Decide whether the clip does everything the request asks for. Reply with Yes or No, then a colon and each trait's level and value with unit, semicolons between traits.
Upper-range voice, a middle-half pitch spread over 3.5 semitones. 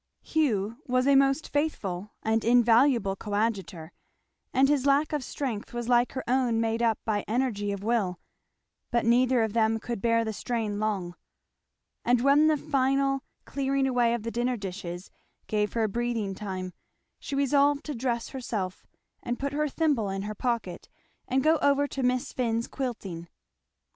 Yes: high, 235 Hz; average, 4.3 semitones